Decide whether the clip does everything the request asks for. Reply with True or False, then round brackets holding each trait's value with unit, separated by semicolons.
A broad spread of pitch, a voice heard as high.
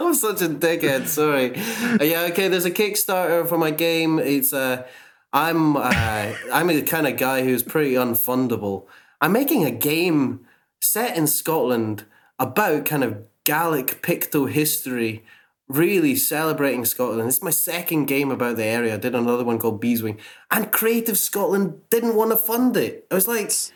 False (6.7 semitones; 150 Hz)